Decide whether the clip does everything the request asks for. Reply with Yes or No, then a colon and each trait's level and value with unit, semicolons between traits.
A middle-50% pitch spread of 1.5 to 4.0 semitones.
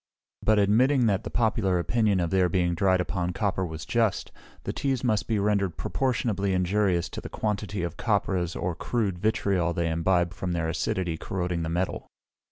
Yes: average, 3.3 semitones